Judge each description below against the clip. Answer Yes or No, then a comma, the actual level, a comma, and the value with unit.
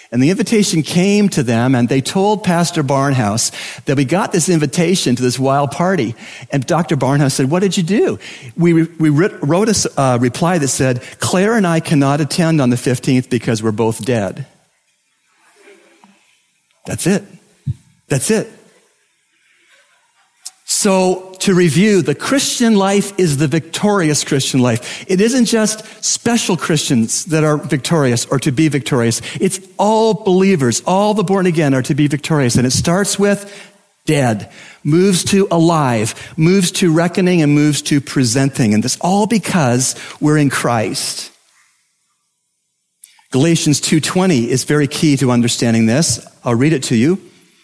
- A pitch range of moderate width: No, wide, 6.0 semitones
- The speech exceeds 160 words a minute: No, average, 155 wpm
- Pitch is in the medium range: Yes, medium, 155 Hz